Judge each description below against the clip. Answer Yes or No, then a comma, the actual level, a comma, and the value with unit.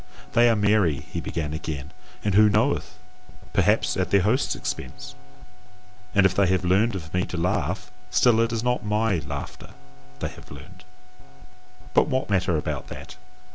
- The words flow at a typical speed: Yes, average, 165 wpm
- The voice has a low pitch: Yes, very low, 95 Hz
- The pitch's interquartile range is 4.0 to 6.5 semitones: Yes, average, 4.6 semitones